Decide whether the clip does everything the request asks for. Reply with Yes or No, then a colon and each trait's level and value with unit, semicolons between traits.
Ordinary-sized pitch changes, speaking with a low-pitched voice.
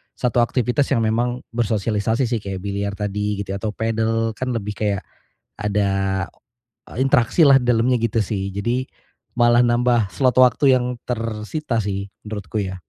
Yes: average, 3.1 semitones; low, 115 Hz